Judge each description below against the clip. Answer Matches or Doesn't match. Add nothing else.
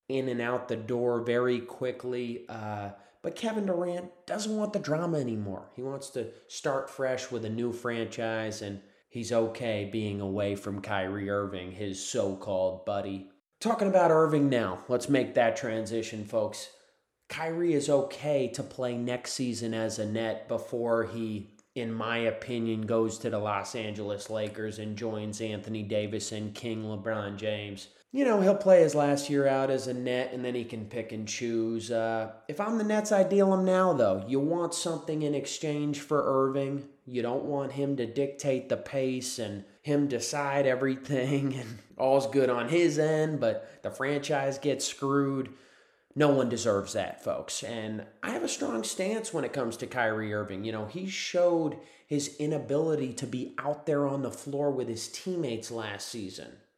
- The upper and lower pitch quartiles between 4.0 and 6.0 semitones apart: Matches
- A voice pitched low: Matches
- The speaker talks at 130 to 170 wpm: Doesn't match